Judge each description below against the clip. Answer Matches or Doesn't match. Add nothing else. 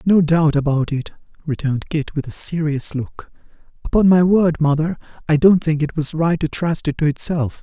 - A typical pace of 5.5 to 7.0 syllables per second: Doesn't match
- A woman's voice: Doesn't match